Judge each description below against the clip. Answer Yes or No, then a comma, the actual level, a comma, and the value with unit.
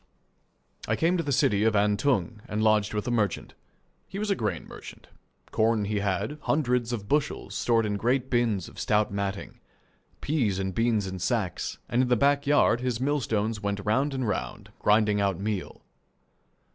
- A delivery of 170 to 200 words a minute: Yes, average, 175 wpm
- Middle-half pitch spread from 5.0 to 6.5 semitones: No, average, 3.8 semitones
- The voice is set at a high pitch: No, low, 110 Hz